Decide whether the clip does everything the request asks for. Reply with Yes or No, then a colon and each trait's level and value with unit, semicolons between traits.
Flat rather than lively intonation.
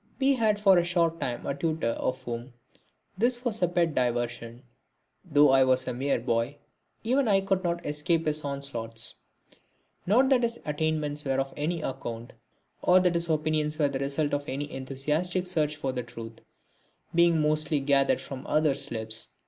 No: average, 4.6 semitones